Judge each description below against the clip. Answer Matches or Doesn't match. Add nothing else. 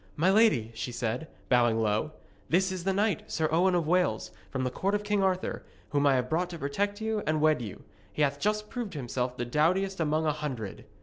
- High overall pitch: Doesn't match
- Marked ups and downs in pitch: Matches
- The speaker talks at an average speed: Doesn't match